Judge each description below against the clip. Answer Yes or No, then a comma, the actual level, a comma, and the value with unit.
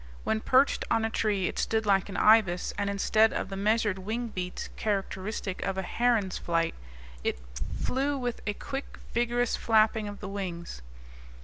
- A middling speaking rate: Yes, average, 170 wpm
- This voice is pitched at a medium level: No, high, 210 Hz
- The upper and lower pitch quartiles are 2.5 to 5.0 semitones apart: Yes, average, 2.9 semitones